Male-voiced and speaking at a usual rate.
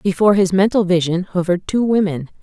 No: female; average, 175 wpm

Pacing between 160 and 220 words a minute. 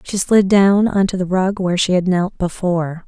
No: fast, 235 wpm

